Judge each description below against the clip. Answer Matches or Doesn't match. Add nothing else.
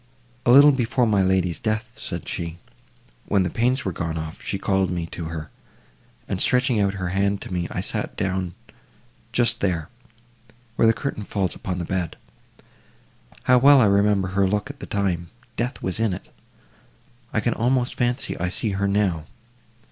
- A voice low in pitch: Matches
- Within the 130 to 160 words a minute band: Doesn't match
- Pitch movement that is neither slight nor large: Matches